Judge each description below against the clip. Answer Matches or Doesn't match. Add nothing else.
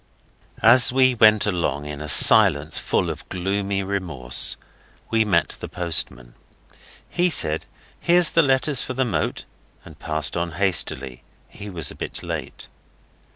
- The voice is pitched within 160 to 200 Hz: Doesn't match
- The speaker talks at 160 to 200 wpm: Doesn't match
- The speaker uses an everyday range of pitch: Doesn't match